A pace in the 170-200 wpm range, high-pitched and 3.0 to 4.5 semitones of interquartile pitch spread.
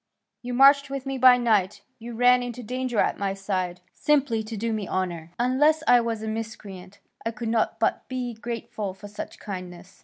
Yes: average, 190 wpm; high, 225 Hz; average, 3.9 semitones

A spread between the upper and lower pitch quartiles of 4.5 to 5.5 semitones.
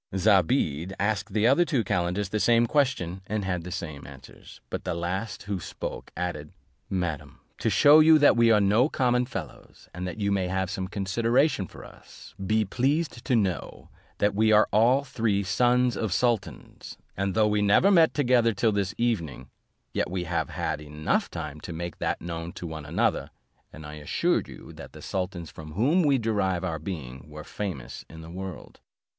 Yes: average, 5.2 semitones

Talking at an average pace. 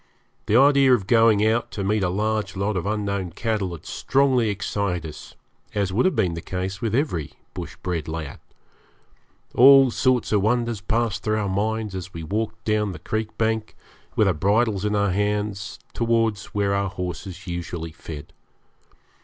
Yes: average, 170 wpm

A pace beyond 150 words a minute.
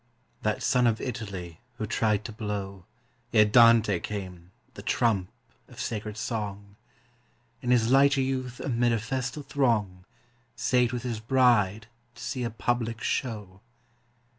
No: average, 140 wpm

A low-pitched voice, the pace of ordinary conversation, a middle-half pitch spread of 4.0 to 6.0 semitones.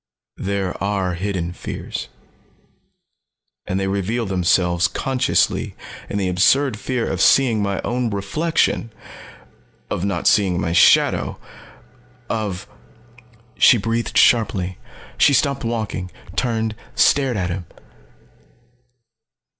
No: low, 105 Hz; slow, 105 wpm; average, 4.4 semitones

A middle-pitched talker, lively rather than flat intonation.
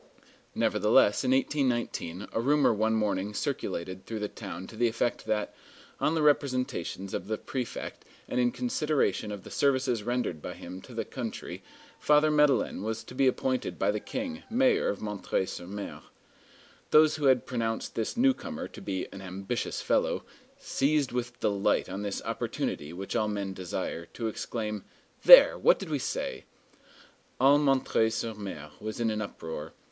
No: low, 115 Hz; wide, 5.8 semitones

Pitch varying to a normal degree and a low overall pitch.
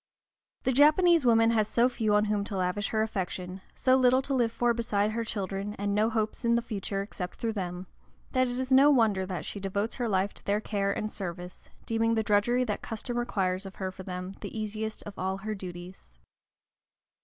No: average, 3.3 semitones; high, 210 Hz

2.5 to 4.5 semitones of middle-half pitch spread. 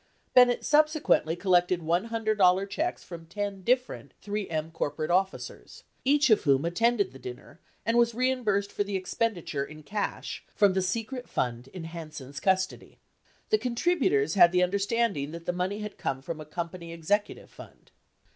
No: wide, 5.5 semitones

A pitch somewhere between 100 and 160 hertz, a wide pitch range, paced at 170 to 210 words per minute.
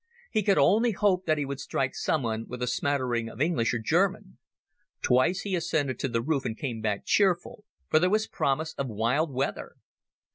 Yes: medium, 140 Hz; wide, 6.4 semitones; average, 190 wpm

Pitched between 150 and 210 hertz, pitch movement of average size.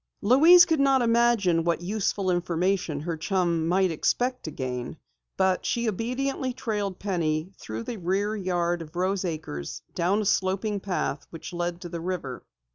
Yes: medium, 185 Hz; average, 4.1 semitones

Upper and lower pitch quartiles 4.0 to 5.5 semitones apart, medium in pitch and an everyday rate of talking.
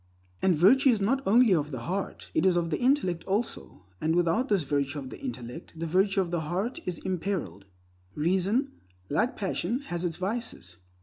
Yes: average, 4.8 semitones; medium, 180 Hz; average, 185 wpm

